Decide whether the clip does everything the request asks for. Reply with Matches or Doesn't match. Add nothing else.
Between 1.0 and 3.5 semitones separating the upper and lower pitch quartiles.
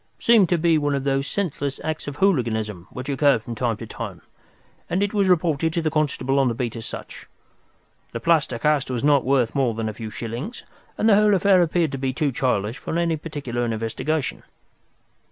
Doesn't match